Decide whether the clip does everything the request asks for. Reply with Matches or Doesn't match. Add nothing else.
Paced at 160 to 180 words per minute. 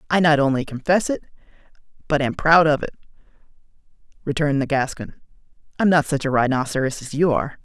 Matches